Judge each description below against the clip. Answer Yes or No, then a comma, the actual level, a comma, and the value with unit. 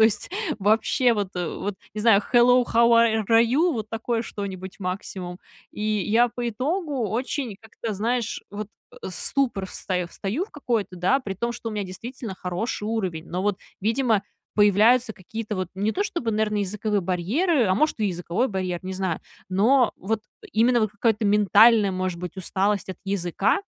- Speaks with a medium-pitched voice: No, high, 210 Hz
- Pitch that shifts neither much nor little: Yes, average, 3.7 semitones